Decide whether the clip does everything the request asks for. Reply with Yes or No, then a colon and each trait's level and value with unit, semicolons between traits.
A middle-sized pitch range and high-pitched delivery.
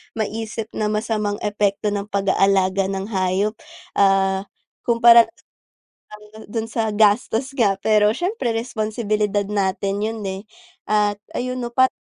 No: narrow, 2.2 semitones; high, 210 Hz